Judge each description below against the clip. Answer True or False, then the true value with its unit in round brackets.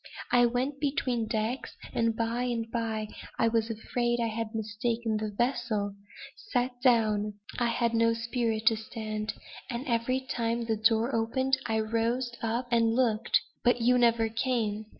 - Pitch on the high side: True (230 Hz)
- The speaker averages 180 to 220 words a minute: False (160 wpm)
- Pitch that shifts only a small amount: True (1.7 semitones)